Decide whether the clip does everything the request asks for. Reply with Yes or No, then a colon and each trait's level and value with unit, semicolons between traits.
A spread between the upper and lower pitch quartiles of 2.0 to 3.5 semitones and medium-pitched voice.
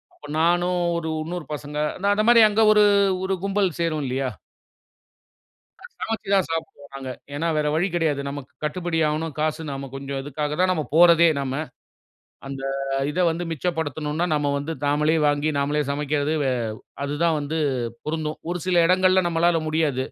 Yes: average, 3.2 semitones; medium, 155 Hz